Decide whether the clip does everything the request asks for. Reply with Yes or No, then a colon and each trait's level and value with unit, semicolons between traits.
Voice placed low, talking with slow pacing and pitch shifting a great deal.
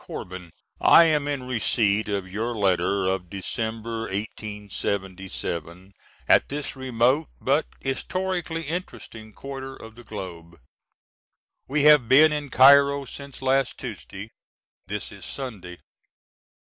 Yes: low, 115 Hz; slow, 115 wpm; wide, 6.0 semitones